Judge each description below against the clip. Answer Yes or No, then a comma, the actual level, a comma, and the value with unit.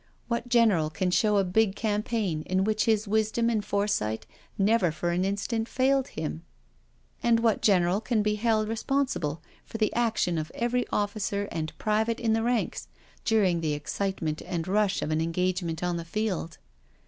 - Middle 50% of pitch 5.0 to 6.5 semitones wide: No, average, 4.3 semitones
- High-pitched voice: Yes, high, 205 Hz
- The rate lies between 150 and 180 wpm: Yes, average, 170 wpm